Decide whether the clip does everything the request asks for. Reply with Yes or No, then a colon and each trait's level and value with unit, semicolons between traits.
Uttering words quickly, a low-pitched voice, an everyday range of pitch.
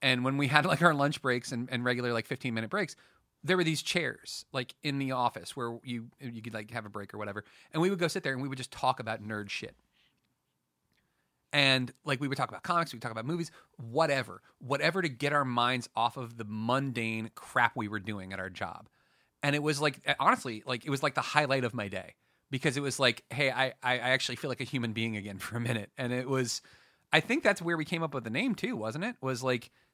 Yes: fast, 250 wpm; low, 130 Hz; average, 3.7 semitones